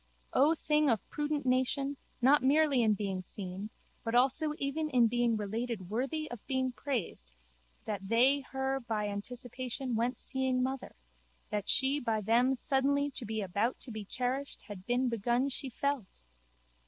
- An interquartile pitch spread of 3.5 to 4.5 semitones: Yes, average, 3.8 semitones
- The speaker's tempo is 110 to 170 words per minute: Yes, average, 155 wpm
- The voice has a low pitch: No, very high, 250 Hz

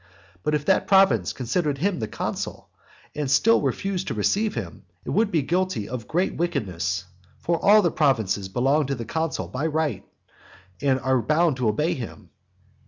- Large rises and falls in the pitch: Yes, wide, 6.3 semitones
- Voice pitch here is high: No, medium, 145 Hz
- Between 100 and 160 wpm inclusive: No, average, 170 wpm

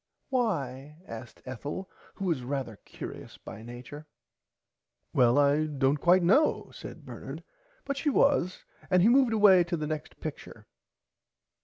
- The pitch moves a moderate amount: No, wide, 6.3 semitones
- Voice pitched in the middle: Yes, medium, 155 Hz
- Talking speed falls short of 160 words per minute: Yes, average, 140 wpm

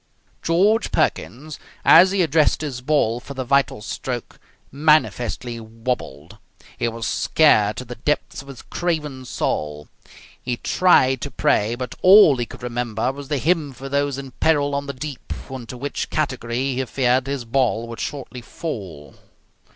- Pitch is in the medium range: No, low, 130 Hz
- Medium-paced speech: Yes, average, 160 wpm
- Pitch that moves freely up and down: No, average, 3.6 semitones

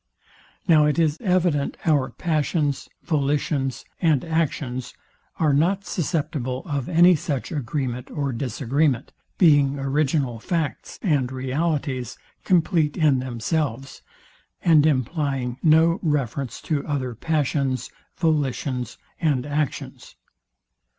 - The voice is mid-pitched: Yes, medium, 145 Hz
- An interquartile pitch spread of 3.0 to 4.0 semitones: Yes, average, 3.4 semitones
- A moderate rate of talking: No, slow, 105 wpm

